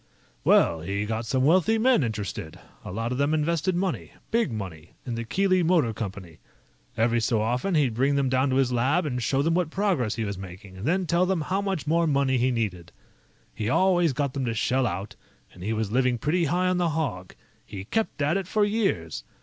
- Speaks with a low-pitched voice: Yes, low, 130 Hz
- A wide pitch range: Yes, wide, 7.5 semitones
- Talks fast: Yes, fast, 215 wpm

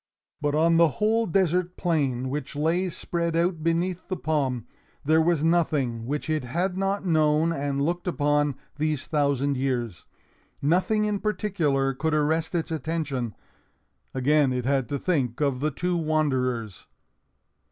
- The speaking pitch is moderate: Yes, medium, 155 Hz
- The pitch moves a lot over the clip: No, average, 3.7 semitones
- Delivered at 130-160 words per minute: Yes, average, 145 wpm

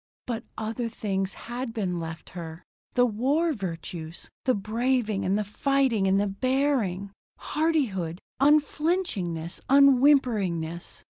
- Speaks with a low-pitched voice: No, high, 220 Hz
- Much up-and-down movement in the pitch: Yes, wide, 6.2 semitones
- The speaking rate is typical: No, slow, 115 wpm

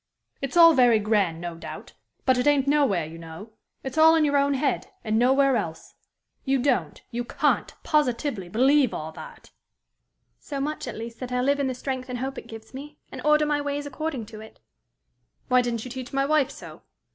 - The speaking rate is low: No, fast, 205 wpm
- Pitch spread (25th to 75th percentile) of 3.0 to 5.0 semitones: Yes, average, 4.3 semitones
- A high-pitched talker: Yes, very high, 260 Hz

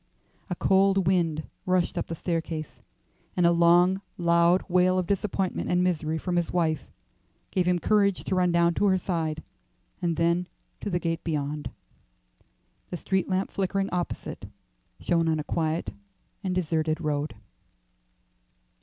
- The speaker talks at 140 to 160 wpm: Yes, average, 145 wpm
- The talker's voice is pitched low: No, medium, 175 Hz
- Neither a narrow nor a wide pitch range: No, narrow, 2.0 semitones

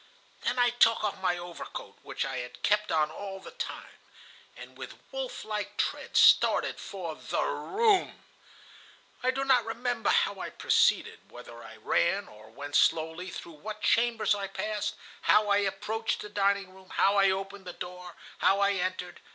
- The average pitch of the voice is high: Yes, high, 200 Hz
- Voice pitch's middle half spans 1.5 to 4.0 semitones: Yes, average, 3.4 semitones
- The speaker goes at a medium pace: Yes, average, 170 wpm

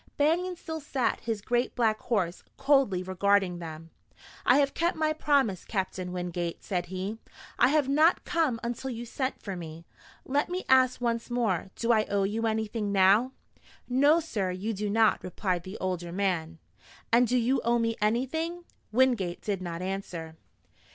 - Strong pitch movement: Yes, wide, 5.8 semitones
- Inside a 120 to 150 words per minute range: No, average, 165 wpm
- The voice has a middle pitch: No, high, 220 Hz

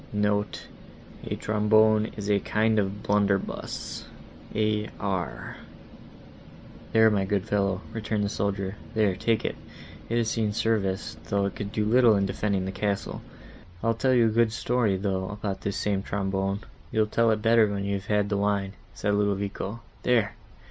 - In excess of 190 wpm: No, average, 155 wpm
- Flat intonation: Yes, narrow, 1.8 semitones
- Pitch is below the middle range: Yes, low, 105 Hz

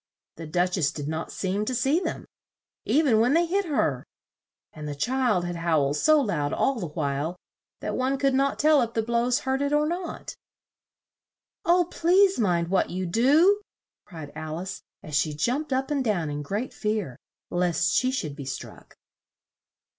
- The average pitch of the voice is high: Yes, high, 215 Hz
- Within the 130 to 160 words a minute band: No, average, 180 wpm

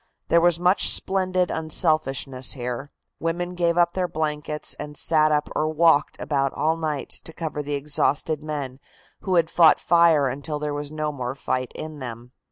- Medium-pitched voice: Yes, medium, 155 Hz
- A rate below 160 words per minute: No, average, 175 wpm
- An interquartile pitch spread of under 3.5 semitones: Yes, average, 2.7 semitones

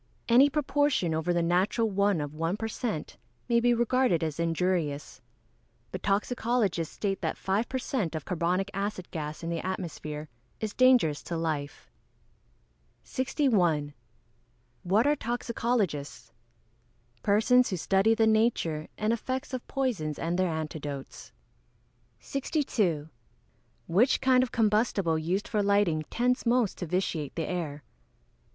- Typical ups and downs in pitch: No, wide, 6.4 semitones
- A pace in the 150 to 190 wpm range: No, slow, 135 wpm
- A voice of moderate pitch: No, high, 195 Hz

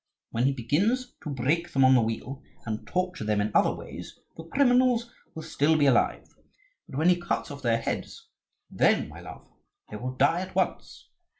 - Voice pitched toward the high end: No, medium, 145 Hz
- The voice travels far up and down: Yes, wide, 6.6 semitones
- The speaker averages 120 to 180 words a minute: No, average, 190 wpm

